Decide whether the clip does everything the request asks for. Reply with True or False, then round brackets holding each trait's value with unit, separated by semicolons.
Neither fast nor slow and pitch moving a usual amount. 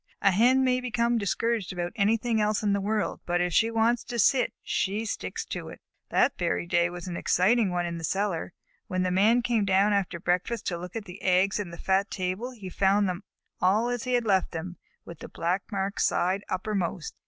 False (215 wpm; 3.9 semitones)